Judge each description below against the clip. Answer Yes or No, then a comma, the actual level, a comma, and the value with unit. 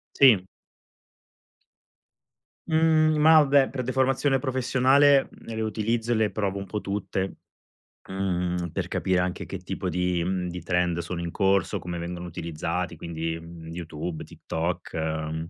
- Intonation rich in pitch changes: Yes, wide, 6.7 semitones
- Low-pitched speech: Yes, very low, 95 Hz